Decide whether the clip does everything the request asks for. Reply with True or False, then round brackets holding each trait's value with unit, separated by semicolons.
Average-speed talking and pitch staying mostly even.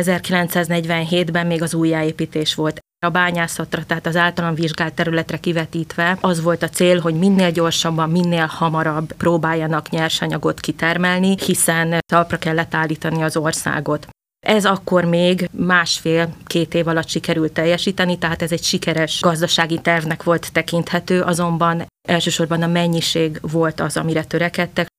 True (130 wpm; 1.3 semitones)